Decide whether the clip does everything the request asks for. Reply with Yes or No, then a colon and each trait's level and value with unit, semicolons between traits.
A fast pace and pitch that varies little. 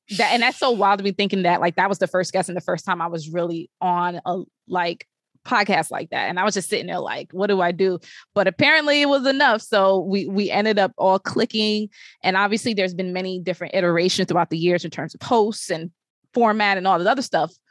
No: fast, 245 wpm; average, 3.1 semitones